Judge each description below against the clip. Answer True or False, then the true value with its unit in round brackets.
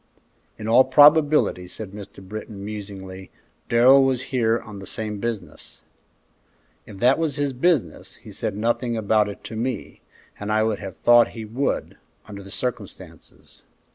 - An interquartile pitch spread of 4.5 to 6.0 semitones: False (3.7 semitones)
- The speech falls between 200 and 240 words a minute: False (155 wpm)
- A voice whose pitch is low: True (110 Hz)